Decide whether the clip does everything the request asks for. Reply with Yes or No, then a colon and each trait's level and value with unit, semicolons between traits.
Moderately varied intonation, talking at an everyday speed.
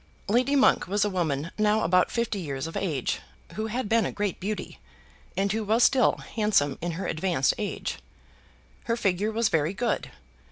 Yes: average, 4.6 semitones; average, 175 wpm